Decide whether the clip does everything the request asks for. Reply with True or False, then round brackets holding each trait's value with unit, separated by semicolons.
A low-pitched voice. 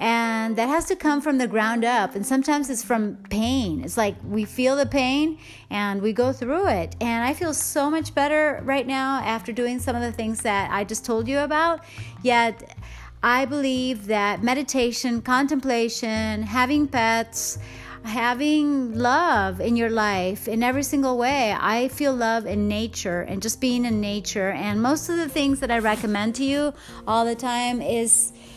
False (240 Hz)